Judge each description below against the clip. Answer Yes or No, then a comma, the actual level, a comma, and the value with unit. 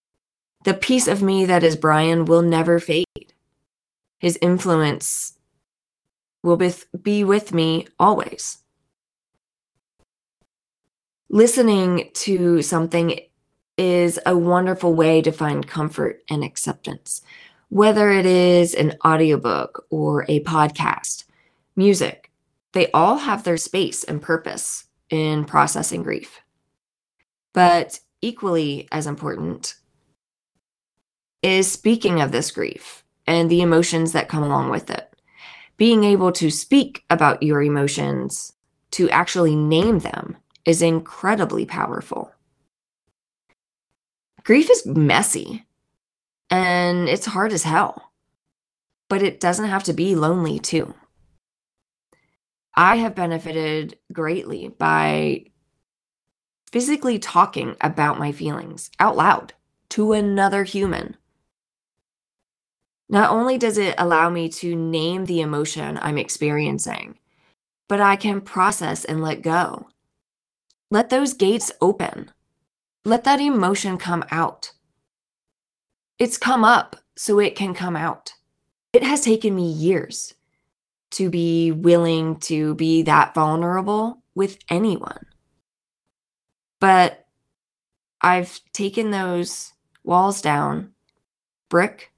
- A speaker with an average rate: No, slow, 110 wpm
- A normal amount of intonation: Yes, average, 3.7 semitones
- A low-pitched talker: No, medium, 175 Hz